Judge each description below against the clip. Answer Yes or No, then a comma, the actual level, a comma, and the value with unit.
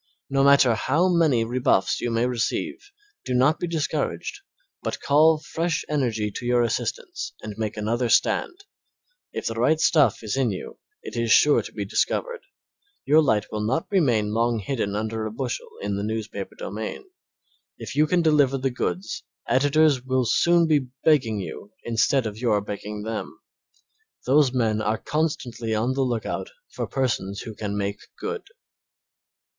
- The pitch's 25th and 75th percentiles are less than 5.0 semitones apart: No, average, 5.3 semitones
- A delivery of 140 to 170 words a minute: Yes, average, 160 wpm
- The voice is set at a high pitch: No, low, 120 Hz